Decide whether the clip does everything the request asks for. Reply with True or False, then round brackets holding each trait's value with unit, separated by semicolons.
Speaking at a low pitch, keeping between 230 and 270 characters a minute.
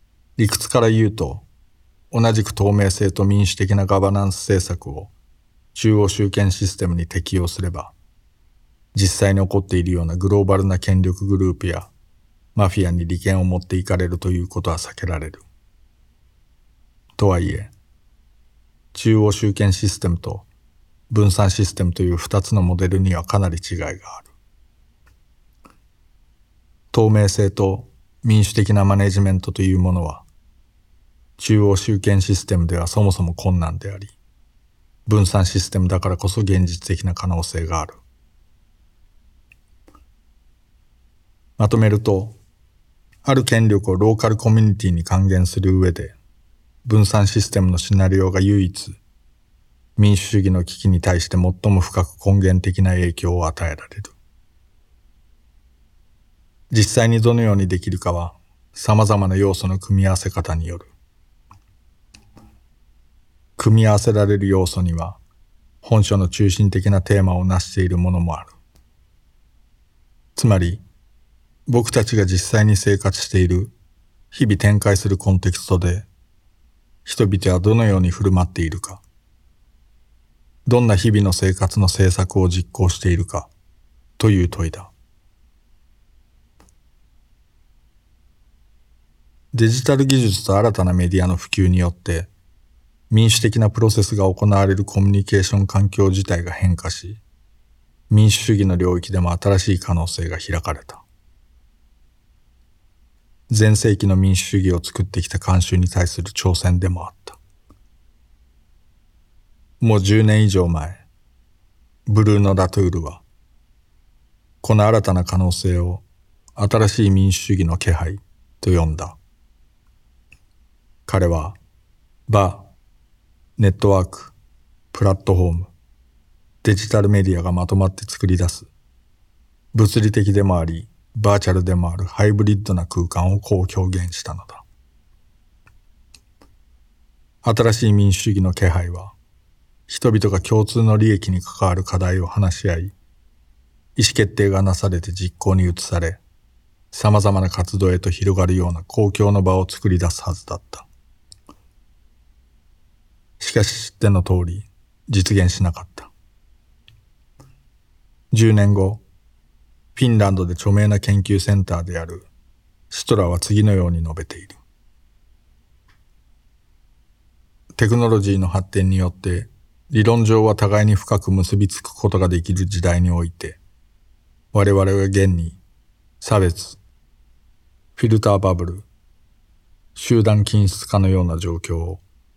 True (95 Hz; 255 characters per minute)